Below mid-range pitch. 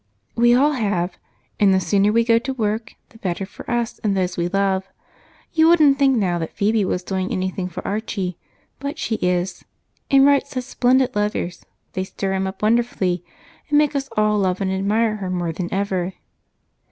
No: high, 205 Hz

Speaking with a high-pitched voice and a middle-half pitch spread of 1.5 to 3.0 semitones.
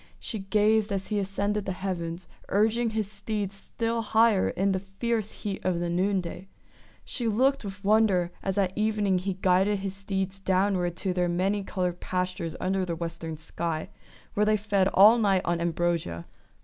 Yes: high, 195 Hz; narrow, 2.5 semitones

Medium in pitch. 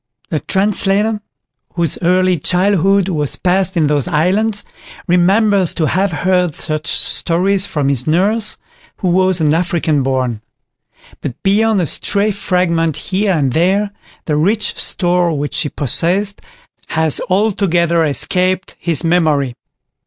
Yes: medium, 180 Hz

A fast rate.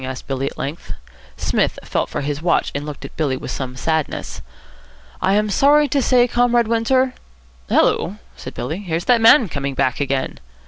No: average, 185 wpm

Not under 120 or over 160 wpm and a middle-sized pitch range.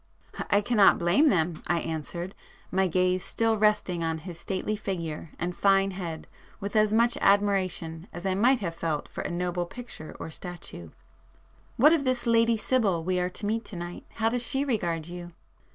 No: average, 175 wpm; average, 4.0 semitones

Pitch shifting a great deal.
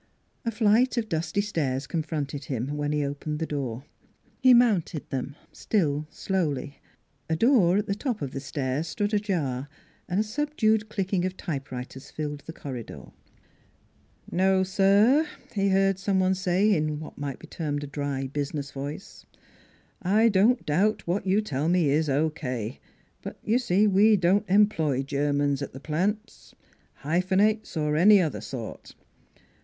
Yes: wide, 6.0 semitones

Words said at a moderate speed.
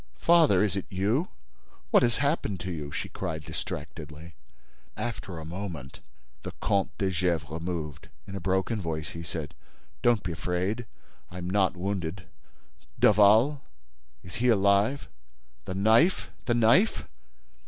No: slow, 120 wpm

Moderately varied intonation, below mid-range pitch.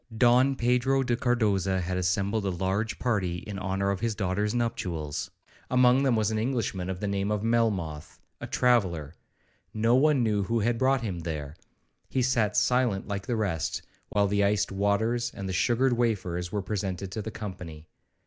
Yes: average, 4.1 semitones; low, 105 Hz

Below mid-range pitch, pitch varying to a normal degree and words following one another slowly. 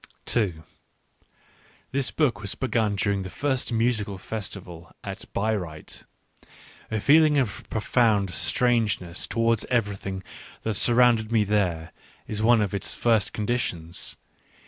Yes: low, 110 Hz; average, 3.4 semitones; slow, 125 wpm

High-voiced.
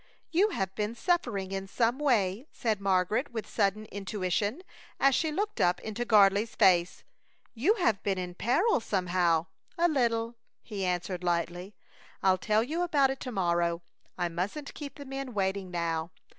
Yes: high, 210 Hz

